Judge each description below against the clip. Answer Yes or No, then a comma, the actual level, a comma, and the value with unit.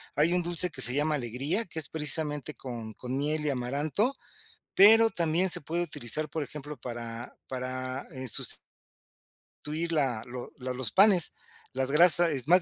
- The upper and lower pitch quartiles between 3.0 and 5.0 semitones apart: Yes, average, 4.6 semitones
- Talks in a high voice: No, medium, 150 Hz